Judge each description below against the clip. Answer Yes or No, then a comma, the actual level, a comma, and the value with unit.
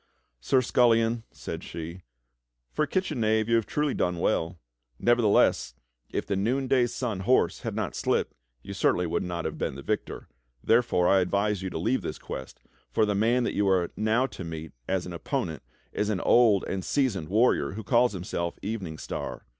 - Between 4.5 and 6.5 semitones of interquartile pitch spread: Yes, average, 4.8 semitones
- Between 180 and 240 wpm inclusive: Yes, average, 185 wpm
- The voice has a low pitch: Yes, low, 100 Hz